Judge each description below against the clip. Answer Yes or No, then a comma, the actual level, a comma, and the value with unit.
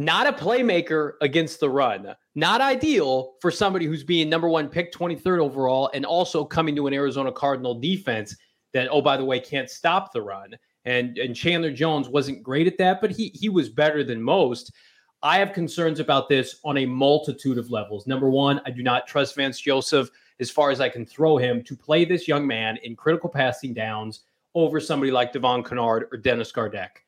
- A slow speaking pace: No, fast, 205 wpm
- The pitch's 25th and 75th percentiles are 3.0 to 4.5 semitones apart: Yes, average, 4.2 semitones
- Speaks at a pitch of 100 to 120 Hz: No, medium, 140 Hz